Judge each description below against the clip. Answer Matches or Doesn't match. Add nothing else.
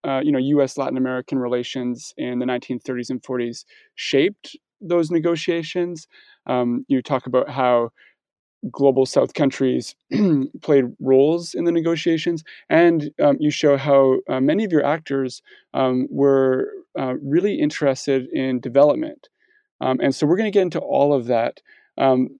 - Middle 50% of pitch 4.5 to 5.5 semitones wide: Matches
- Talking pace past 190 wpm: Doesn't match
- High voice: Doesn't match